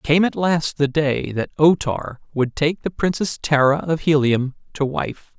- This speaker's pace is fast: No, average, 190 wpm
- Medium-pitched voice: Yes, medium, 150 Hz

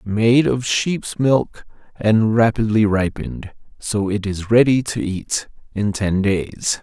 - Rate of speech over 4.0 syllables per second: No, 3.5 syllables/s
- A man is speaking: Yes, male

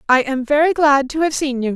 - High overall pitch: Yes, very high, 280 Hz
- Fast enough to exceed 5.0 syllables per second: Yes, 5.6 syllables/s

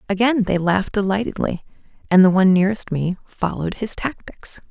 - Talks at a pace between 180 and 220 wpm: No, average, 155 wpm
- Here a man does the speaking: No, female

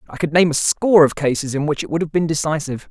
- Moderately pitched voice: Yes, medium, 155 Hz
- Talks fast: Yes, fast, 290 wpm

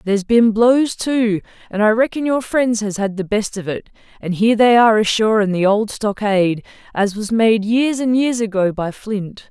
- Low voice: No, high, 215 Hz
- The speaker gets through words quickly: Yes, fast, 210 wpm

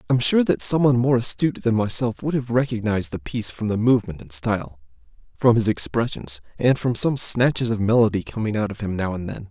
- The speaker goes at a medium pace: No, fast, 215 wpm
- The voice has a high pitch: No, low, 115 Hz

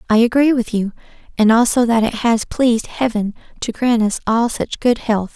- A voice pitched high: Yes, high, 230 Hz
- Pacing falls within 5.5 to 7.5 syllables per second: No, 5.0 syllables/s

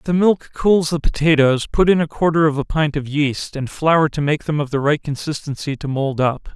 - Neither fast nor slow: No, fast, 245 wpm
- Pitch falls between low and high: Yes, medium, 150 Hz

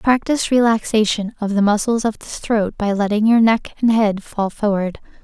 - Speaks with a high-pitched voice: Yes, high, 215 Hz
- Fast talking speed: No, average, 185 wpm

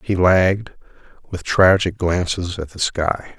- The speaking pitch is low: Yes, very low, 90 Hz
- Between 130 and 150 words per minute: Yes, average, 140 wpm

